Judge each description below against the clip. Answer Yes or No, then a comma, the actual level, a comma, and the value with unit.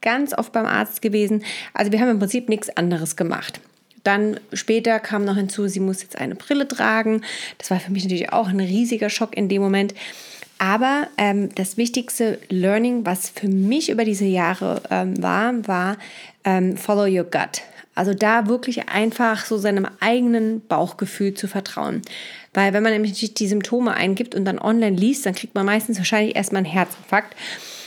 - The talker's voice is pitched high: Yes, high, 210 Hz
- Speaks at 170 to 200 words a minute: Yes, average, 180 wpm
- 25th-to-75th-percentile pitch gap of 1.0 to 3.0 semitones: Yes, average, 2.7 semitones